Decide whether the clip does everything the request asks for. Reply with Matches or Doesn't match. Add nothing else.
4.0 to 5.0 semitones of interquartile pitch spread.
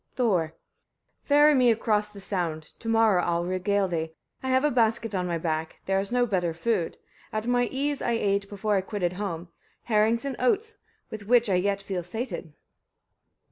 Matches